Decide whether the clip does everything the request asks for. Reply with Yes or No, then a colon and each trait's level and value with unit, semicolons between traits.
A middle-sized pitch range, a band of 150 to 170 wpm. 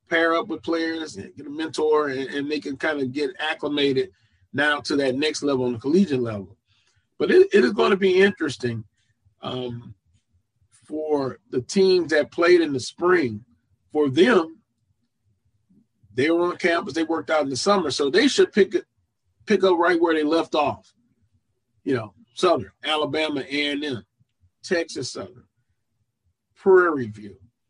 No: wide, 6.6 semitones; average, 160 wpm